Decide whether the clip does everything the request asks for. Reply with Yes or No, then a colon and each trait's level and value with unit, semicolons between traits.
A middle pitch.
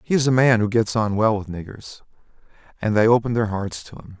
No: low, 110 Hz